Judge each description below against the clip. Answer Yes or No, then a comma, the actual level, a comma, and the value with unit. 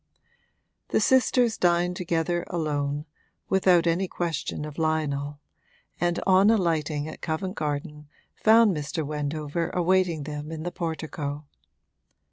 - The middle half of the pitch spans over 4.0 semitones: No, average, 3.0 semitones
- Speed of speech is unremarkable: No, slow, 115 wpm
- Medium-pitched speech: Yes, medium, 160 Hz